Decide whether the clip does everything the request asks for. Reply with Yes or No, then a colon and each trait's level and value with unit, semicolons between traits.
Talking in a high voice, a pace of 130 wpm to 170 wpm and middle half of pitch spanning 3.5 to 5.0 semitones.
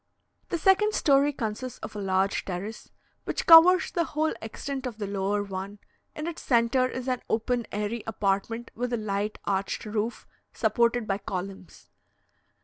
Yes: high, 225 Hz; average, 155 wpm; average, 4.4 semitones